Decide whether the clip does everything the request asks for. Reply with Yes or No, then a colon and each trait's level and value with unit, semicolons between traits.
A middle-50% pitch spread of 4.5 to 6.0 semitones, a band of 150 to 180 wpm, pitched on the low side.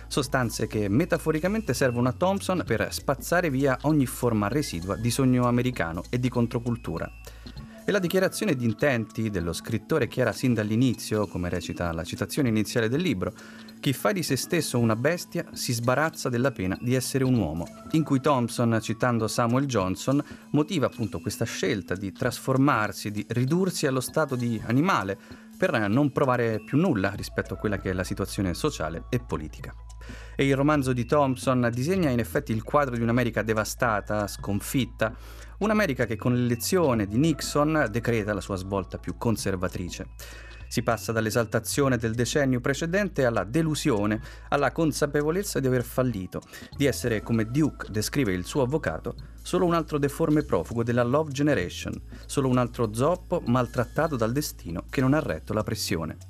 Yes: wide, 5.4 semitones; average, 160 wpm; low, 120 Hz